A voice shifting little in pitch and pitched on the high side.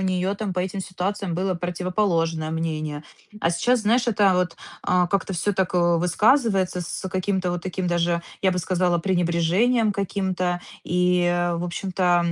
No: narrow, 2.0 semitones; medium, 180 Hz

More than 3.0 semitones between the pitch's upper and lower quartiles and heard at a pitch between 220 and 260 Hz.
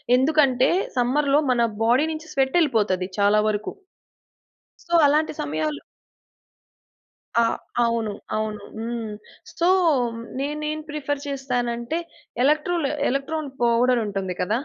Yes: average, 5.2 semitones; very high, 250 Hz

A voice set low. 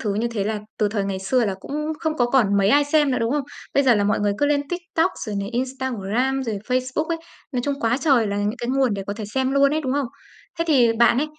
No: very high, 250 Hz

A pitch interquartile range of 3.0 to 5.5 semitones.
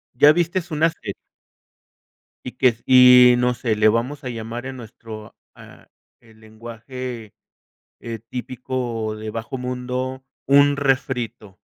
No: narrow, 2.5 semitones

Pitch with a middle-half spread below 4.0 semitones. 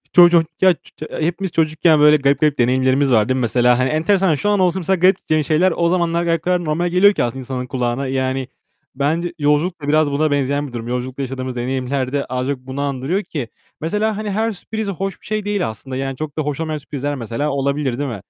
No: average, 4.7 semitones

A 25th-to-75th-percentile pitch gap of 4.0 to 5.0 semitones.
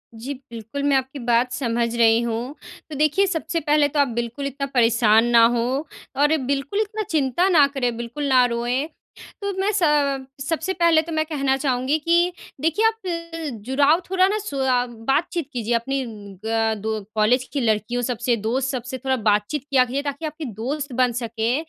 Yes: average, 4.4 semitones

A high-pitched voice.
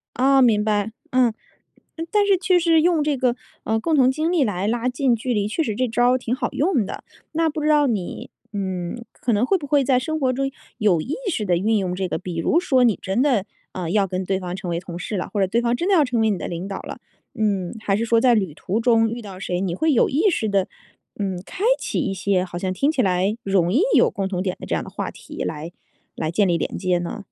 Yes: high, 220 Hz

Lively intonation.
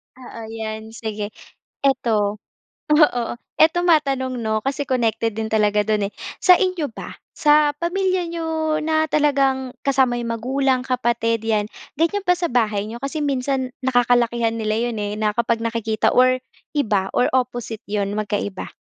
No: average, 4.7 semitones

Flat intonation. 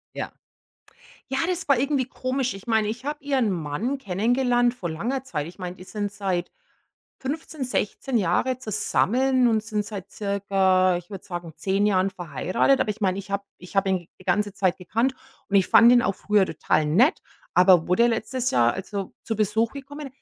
No: average, 5.2 semitones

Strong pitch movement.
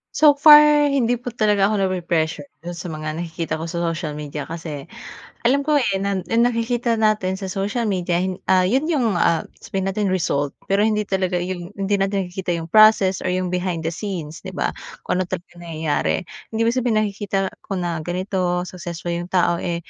No: average, 3.7 semitones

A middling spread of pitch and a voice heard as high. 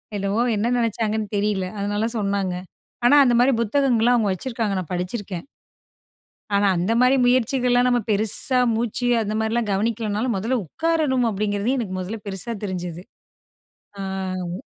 Yes: average, 3.5 semitones; high, 220 Hz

